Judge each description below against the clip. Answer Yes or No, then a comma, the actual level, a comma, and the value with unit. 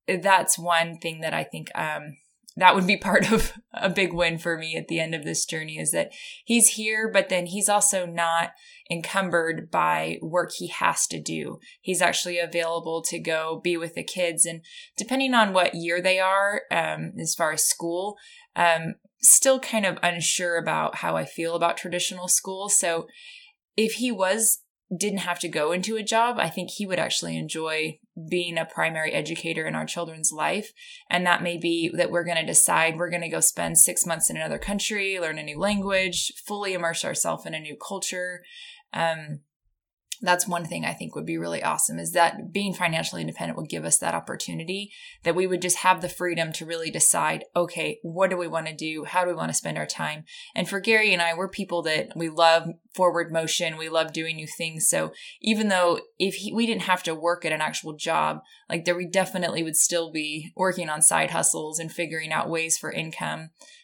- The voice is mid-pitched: Yes, medium, 175 Hz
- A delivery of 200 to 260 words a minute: Yes, fast, 205 wpm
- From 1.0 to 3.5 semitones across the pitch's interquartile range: Yes, average, 3.1 semitones